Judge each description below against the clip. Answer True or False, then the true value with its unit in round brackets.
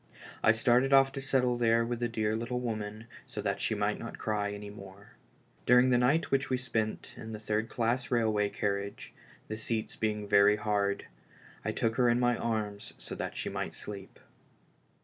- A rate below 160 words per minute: False (190 wpm)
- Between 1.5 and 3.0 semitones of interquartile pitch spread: True (2.7 semitones)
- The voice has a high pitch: False (110 Hz)